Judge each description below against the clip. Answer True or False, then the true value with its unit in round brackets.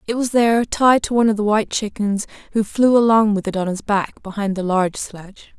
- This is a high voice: True (210 Hz)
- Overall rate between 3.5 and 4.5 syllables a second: False (5.8 syllables/s)